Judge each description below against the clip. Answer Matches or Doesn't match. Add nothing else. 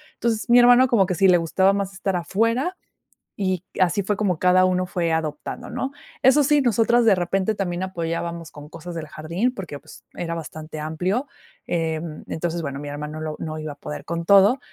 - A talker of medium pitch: Matches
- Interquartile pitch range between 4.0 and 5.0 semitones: Matches